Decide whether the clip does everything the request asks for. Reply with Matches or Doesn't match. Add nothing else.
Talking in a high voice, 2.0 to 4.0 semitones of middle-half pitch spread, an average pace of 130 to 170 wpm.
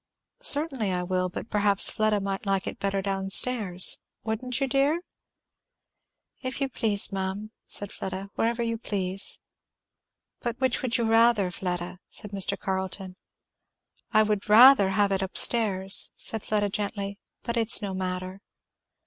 Matches